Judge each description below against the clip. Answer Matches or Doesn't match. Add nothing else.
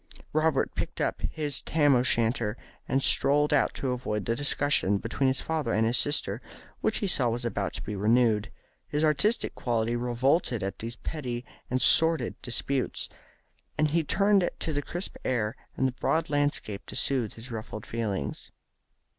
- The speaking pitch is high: Doesn't match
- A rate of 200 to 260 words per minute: Doesn't match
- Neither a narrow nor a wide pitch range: Matches